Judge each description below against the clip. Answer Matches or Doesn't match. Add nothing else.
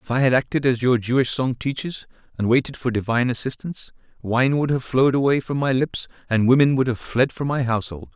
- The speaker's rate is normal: Doesn't match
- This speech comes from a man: Matches